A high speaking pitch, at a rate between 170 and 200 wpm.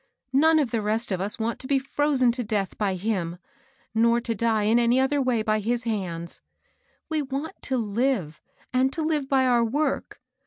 Yes: high, 235 Hz; average, 195 wpm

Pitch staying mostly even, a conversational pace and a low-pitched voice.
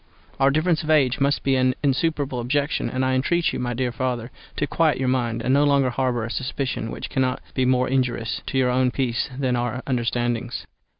No: narrow, 2.0 semitones; fast, 215 wpm; low, 130 Hz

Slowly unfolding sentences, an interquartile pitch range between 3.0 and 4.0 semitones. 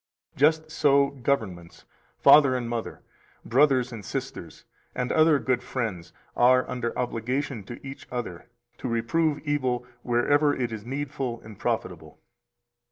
Yes: slow, 130 wpm; average, 3.3 semitones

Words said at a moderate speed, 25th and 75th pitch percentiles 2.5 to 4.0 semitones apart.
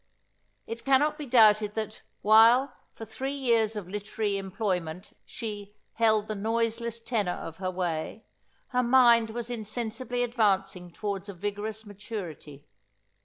No: slow, 130 wpm; average, 2.8 semitones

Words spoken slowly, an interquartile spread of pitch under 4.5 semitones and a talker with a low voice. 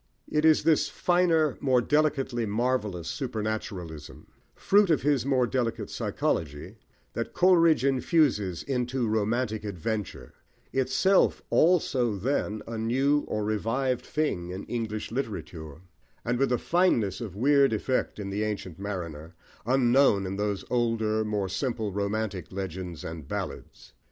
No: slow, 130 wpm; average, 5.1 semitones; low, 115 Hz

